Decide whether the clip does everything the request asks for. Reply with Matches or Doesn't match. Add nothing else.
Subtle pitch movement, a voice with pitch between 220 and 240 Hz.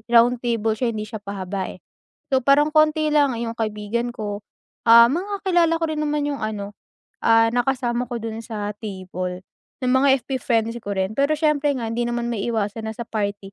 Doesn't match